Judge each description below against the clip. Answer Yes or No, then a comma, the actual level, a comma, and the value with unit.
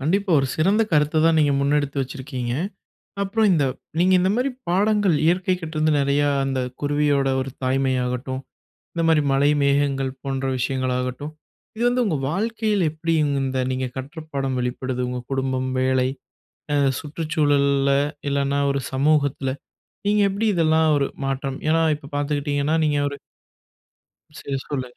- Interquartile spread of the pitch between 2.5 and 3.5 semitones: Yes, average, 3.2 semitones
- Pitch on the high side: No, medium, 145 Hz